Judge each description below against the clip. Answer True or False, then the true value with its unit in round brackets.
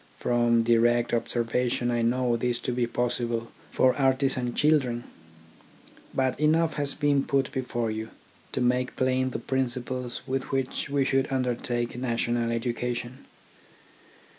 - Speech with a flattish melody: True (1.8 semitones)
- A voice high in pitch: False (125 Hz)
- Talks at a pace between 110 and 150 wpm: True (135 wpm)